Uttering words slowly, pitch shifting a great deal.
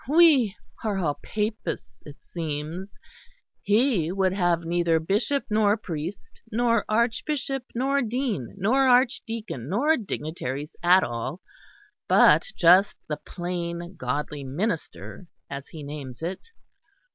Yes: slow, 115 wpm; wide, 6.6 semitones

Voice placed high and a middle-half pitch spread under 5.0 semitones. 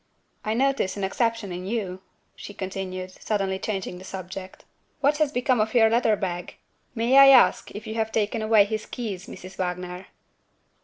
Yes: high, 210 Hz; average, 3.5 semitones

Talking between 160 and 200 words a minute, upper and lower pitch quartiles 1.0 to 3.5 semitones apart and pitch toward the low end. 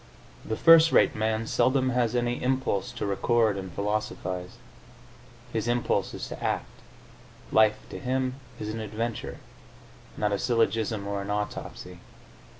No: average, 140 wpm; average, 2.9 semitones; low, 110 Hz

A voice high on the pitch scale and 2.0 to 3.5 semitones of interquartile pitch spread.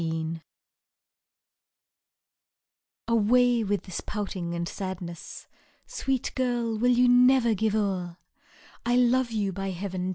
No: high, 210 Hz; average, 4.9 semitones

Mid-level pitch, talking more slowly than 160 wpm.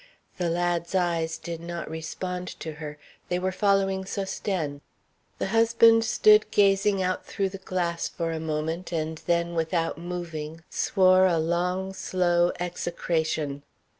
Yes: medium, 175 Hz; slow, 135 wpm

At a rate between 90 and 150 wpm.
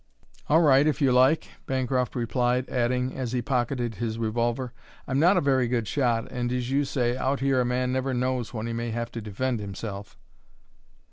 No: average, 195 wpm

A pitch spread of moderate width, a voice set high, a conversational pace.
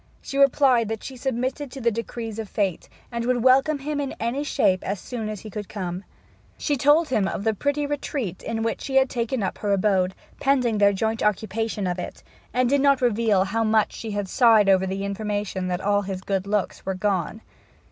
No: average, 4.4 semitones; high, 220 Hz; fast, 210 wpm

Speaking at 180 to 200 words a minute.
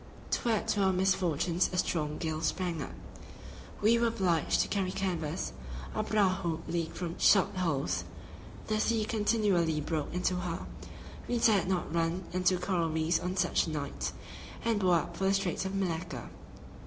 No: average, 170 wpm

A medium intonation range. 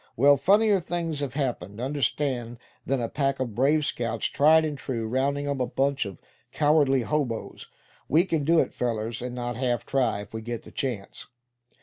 Yes: average, 3.6 semitones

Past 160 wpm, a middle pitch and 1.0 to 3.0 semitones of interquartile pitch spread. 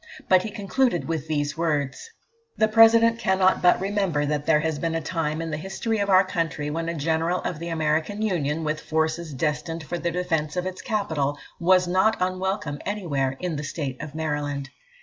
No: average, 190 wpm; medium, 165 Hz; average, 3.7 semitones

